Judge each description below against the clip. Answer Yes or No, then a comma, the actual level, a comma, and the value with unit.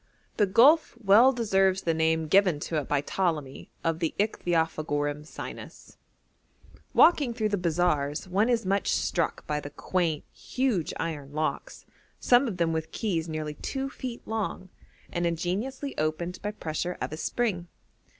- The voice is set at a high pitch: No, medium, 175 Hz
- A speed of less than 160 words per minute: Yes, average, 150 wpm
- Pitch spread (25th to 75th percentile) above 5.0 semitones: Yes, wide, 5.4 semitones